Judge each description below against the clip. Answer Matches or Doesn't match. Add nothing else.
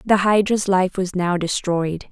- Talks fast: Doesn't match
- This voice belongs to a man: Doesn't match